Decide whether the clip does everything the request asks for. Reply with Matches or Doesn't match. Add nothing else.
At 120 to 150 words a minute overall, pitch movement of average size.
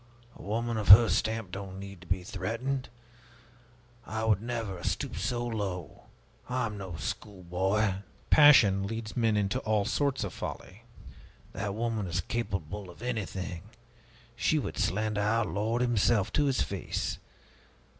Matches